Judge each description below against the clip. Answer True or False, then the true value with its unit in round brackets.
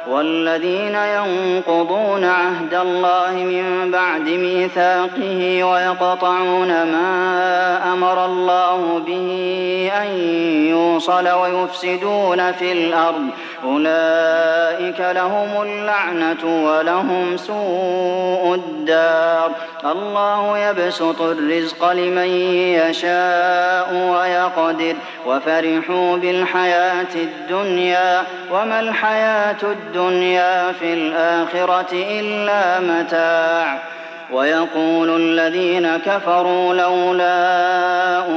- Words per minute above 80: False (70 wpm)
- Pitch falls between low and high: True (180 Hz)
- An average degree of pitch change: False (1.6 semitones)